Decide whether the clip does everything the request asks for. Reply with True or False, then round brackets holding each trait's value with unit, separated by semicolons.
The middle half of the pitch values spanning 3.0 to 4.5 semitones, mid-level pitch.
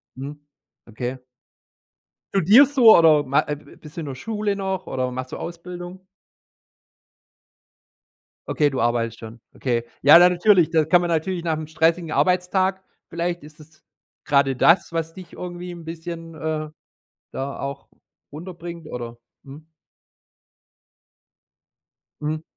True (3.7 semitones; 160 Hz)